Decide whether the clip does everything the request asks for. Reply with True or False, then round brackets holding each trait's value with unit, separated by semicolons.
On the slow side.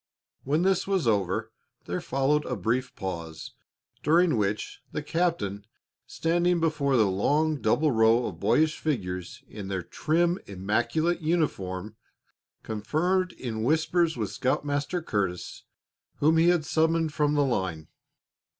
True (130 wpm)